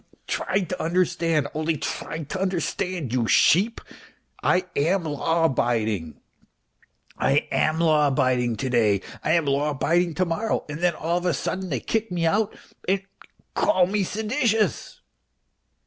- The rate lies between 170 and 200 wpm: No, average, 150 wpm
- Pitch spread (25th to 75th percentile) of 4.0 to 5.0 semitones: Yes, average, 4.5 semitones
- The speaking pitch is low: No, medium, 165 Hz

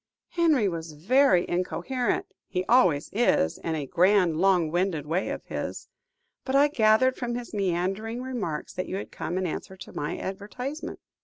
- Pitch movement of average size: No, wide, 6.0 semitones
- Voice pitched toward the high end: Yes, high, 195 Hz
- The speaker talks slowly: No, average, 170 wpm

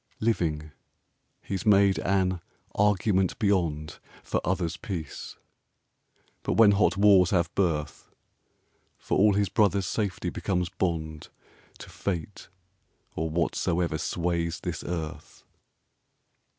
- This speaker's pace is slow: Yes, slow, 105 wpm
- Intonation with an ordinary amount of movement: Yes, average, 3.2 semitones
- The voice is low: Yes, very low, 90 Hz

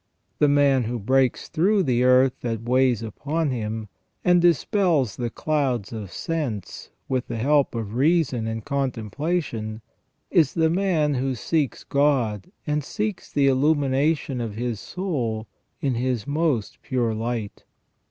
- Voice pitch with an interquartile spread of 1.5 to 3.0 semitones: No, average, 4.6 semitones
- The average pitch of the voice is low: Yes, low, 130 Hz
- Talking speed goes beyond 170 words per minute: No, average, 140 wpm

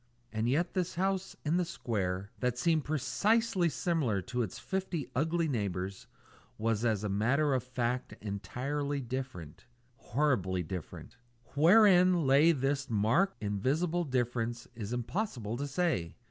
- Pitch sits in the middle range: No, low, 130 Hz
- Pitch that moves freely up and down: Yes, wide, 7.0 semitones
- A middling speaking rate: No, slow, 130 wpm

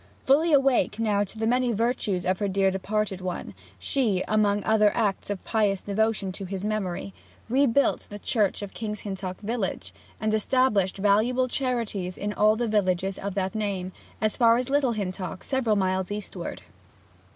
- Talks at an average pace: Yes, average, 170 wpm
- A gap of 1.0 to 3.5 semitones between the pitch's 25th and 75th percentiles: Yes, average, 3.1 semitones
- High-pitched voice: Yes, high, 210 Hz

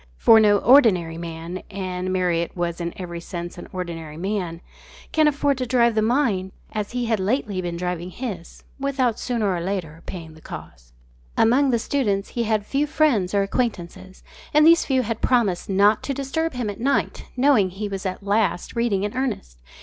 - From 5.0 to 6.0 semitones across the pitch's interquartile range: Yes, wide, 5.6 semitones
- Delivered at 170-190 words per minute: Yes, average, 185 wpm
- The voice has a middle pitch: No, high, 200 Hz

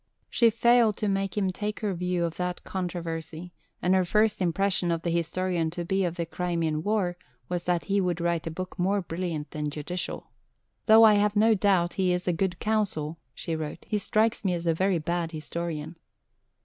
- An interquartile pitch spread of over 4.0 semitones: No, average, 2.9 semitones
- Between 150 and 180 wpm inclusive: No, average, 200 wpm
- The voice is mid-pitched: Yes, medium, 180 Hz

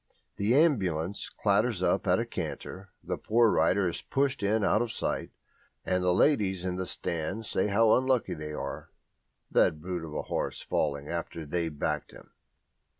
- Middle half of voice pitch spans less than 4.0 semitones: No, average, 5.1 semitones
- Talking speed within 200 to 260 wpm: No, average, 170 wpm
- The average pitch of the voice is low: Yes, very low, 95 Hz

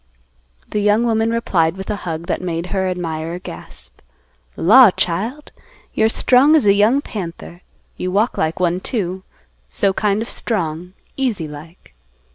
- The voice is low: No, high, 190 Hz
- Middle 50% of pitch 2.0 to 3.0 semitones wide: No, average, 4.6 semitones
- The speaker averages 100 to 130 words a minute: No, average, 150 wpm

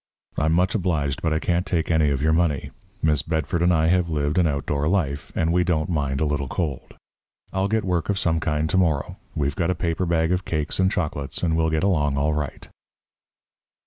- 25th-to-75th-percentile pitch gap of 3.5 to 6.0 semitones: No, average, 3.0 semitones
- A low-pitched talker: Yes, very low, 80 Hz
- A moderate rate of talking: No, fast, 215 wpm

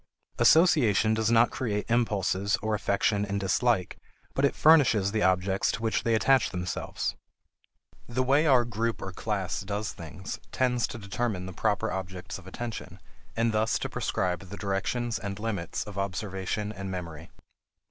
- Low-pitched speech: Yes, low, 105 Hz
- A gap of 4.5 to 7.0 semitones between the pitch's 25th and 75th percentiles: No, average, 3.5 semitones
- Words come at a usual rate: Yes, average, 160 wpm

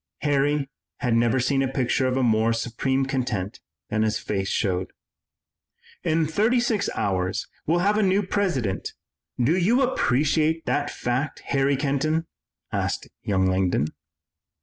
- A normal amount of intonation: No, wide, 5.9 semitones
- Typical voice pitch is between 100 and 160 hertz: Yes, low, 135 Hz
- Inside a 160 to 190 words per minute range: No, slow, 135 wpm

